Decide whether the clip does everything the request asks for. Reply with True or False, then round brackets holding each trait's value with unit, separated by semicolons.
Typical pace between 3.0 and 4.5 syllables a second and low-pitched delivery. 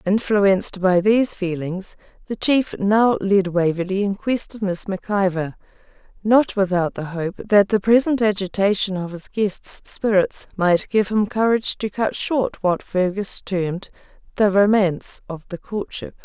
False (4.3 syllables/s; 195 Hz)